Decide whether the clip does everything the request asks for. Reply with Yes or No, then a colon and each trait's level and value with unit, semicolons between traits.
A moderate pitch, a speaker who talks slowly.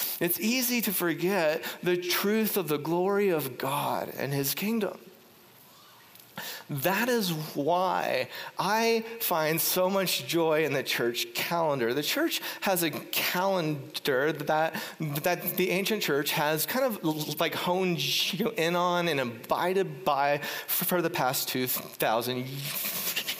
Yes: medium, 175 Hz; slow, 130 wpm